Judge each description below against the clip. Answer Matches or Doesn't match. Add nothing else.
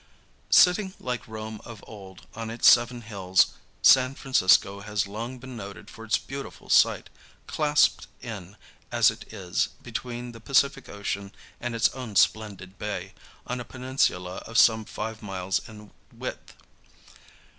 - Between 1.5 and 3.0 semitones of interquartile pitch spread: Doesn't match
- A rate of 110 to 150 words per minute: Matches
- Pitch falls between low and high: Doesn't match